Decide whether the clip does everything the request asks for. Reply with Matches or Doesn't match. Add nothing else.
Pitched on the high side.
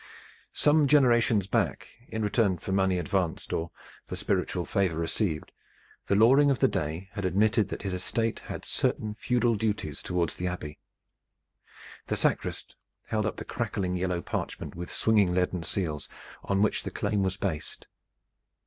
Doesn't match